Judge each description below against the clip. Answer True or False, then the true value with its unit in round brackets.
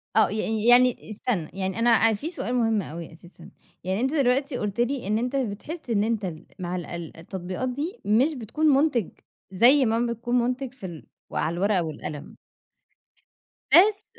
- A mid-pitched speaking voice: False (225 Hz)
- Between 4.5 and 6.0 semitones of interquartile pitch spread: True (5.1 semitones)